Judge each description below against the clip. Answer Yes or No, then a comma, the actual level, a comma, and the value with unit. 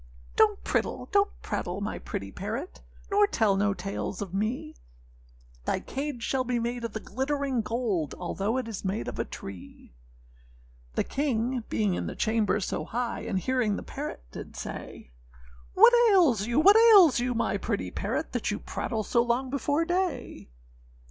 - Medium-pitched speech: No, high, 235 Hz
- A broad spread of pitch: Yes, wide, 5.7 semitones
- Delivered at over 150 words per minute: Yes, average, 170 wpm